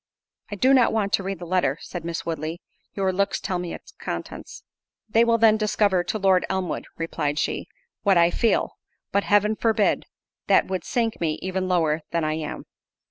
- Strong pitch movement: No, average, 3.8 semitones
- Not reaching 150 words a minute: No, average, 185 wpm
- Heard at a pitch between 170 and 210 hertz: Yes, high, 190 Hz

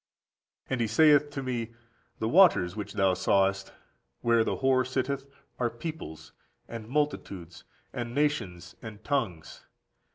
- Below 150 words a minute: Yes, slow, 135 wpm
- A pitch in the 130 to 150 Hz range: No, low, 120 Hz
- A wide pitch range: Yes, wide, 5.8 semitones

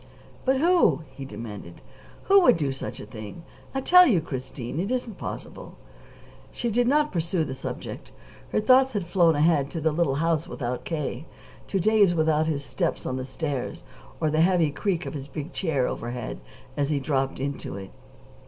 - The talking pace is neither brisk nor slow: Yes, average, 180 wpm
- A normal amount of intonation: No, wide, 6.0 semitones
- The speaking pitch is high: No, medium, 155 Hz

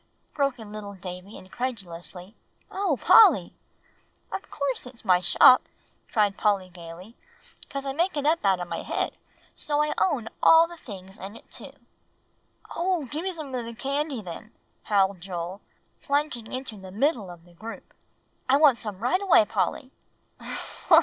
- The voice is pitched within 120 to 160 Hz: No, high, 230 Hz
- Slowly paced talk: No, average, 160 wpm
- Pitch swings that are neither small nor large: No, wide, 7.1 semitones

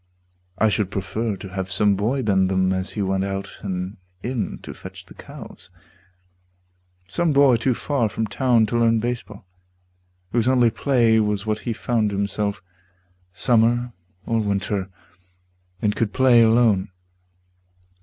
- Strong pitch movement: No, average, 3.2 semitones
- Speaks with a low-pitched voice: Yes, low, 110 Hz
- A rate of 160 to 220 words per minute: No, average, 145 wpm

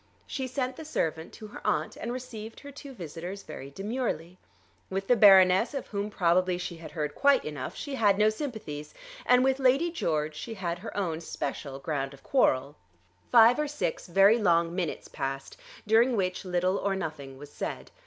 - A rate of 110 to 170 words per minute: No, average, 185 wpm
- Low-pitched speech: No, high, 190 Hz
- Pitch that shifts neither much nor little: No, wide, 7.0 semitones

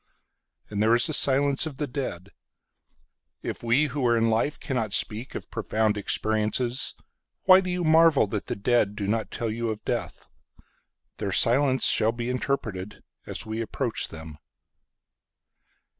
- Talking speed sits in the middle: No, slow, 130 wpm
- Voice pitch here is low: Yes, low, 115 Hz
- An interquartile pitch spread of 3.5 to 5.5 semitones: Yes, average, 4.4 semitones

